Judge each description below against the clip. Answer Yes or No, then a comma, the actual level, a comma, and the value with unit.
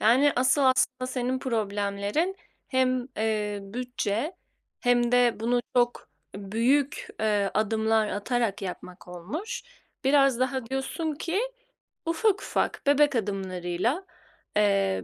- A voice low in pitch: No, high, 240 Hz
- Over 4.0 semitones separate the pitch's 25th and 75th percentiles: Yes, average, 4.4 semitones